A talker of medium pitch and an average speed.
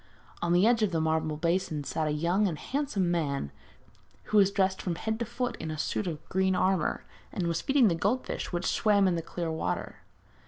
No: medium, 180 Hz; fast, 210 wpm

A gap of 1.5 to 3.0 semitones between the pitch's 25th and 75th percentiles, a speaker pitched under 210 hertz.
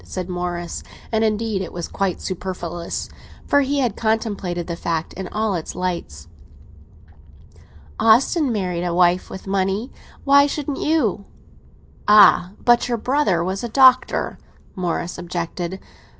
No: average, 4.6 semitones; high, 190 Hz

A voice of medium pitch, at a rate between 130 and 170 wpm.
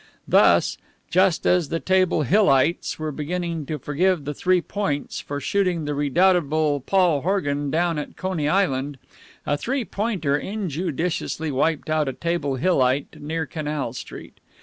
Yes: medium, 160 Hz; average, 145 wpm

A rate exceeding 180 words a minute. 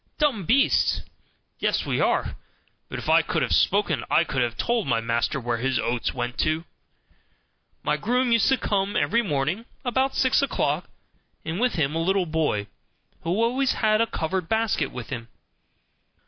No: average, 170 wpm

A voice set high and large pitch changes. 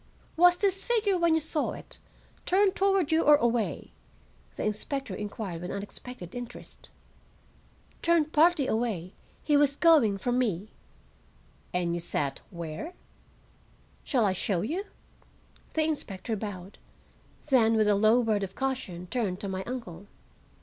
Yes: high, 235 Hz; wide, 8.0 semitones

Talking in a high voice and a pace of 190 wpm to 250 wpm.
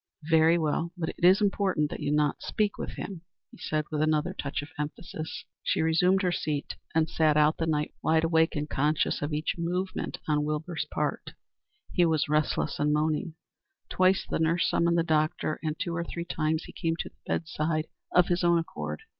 No: medium, 160 Hz; fast, 205 wpm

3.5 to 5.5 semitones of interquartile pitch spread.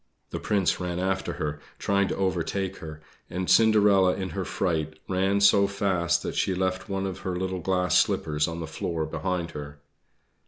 No: narrow, 2.5 semitones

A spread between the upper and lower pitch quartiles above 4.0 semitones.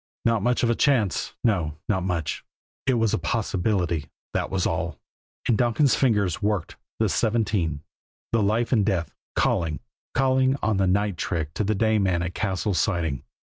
Yes: average, 4.5 semitones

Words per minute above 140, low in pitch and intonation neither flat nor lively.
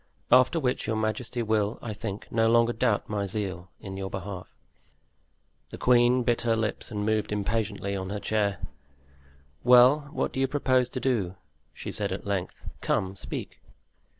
Yes: average, 165 wpm; low, 110 Hz; average, 3.4 semitones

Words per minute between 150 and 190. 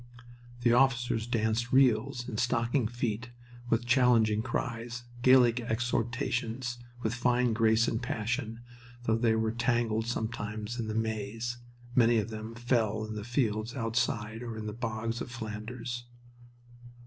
No: slow, 135 wpm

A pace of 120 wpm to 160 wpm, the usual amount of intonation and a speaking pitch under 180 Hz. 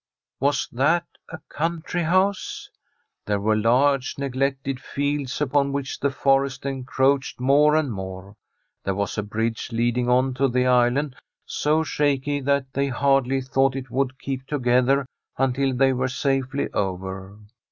No: average, 140 wpm; narrow, 2.2 semitones; low, 135 Hz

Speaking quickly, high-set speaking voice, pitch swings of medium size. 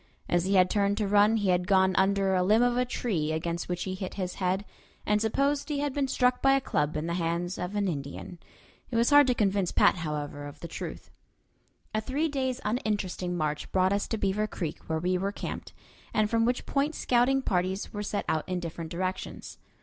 Yes: fast, 220 wpm; high, 195 Hz; average, 4.5 semitones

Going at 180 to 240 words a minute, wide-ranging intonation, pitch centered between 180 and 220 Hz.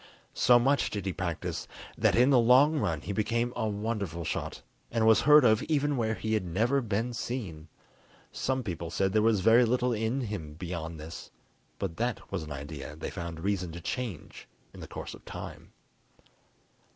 No: average, 185 wpm; wide, 6.1 semitones; low, 110 Hz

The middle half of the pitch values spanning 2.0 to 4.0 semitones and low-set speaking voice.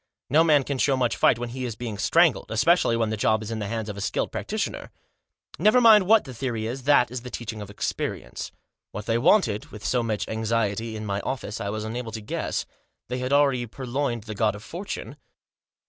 Yes: average, 3.5 semitones; low, 115 Hz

